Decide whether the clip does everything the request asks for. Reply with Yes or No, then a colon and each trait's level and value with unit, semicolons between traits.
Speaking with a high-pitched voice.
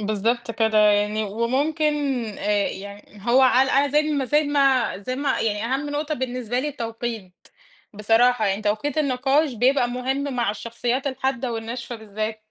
Yes: high, 245 Hz